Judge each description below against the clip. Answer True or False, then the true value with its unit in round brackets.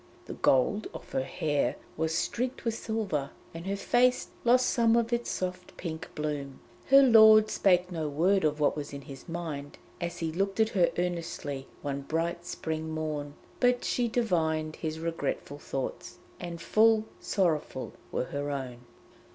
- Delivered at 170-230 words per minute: False (160 wpm)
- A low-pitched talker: False (165 Hz)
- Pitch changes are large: True (6.4 semitones)